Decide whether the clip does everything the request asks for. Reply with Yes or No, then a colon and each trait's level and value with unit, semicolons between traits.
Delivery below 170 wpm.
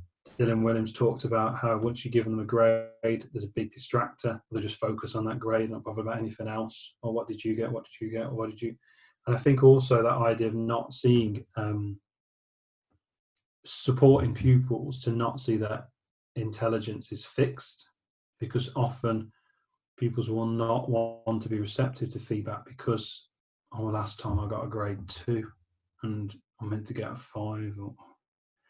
No: average, 180 wpm